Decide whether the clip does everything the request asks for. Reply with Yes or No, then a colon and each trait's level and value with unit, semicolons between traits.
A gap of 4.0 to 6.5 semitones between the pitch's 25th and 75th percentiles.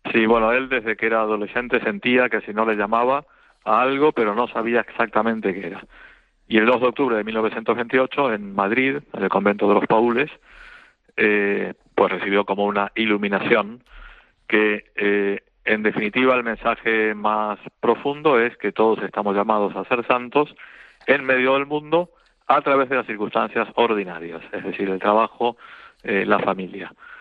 No: average, 3.5 semitones